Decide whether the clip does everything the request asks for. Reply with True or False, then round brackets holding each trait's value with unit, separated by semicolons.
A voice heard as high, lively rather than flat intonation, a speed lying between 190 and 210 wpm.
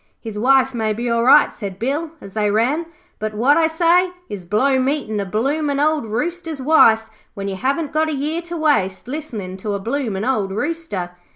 True (255 Hz; 6.4 semitones; 195 wpm)